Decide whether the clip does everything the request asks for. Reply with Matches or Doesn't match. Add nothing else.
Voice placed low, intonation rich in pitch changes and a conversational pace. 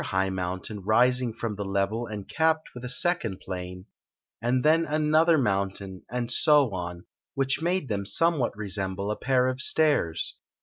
Matches